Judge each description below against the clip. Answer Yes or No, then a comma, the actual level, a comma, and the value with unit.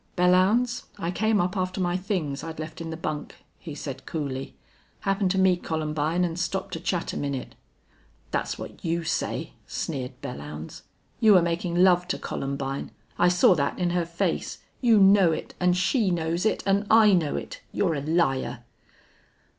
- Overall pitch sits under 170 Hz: No, medium, 175 Hz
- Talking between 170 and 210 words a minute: Yes, average, 175 wpm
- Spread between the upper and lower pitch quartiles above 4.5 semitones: No, average, 3.5 semitones